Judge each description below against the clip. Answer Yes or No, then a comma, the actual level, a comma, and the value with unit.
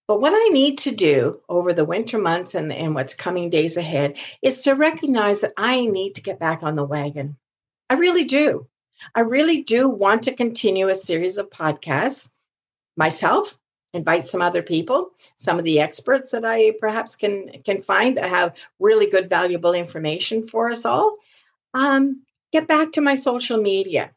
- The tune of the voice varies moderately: No, wide, 7.6 semitones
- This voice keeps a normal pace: Yes, average, 180 wpm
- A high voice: Yes, high, 205 Hz